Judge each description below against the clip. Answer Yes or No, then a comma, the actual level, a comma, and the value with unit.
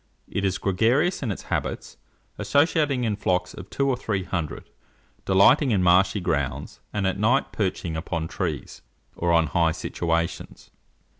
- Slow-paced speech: No, average, 150 wpm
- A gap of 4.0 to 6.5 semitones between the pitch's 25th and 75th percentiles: Yes, average, 5.2 semitones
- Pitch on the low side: Yes, very low, 95 Hz